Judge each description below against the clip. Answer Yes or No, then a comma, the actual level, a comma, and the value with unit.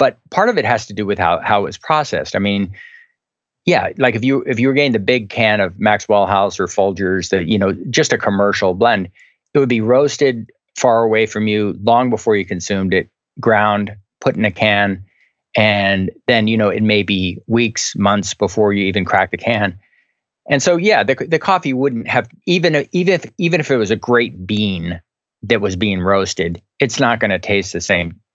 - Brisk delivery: Yes, fast, 215 wpm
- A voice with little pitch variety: No, average, 4.4 semitones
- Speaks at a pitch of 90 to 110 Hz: Yes, low, 105 Hz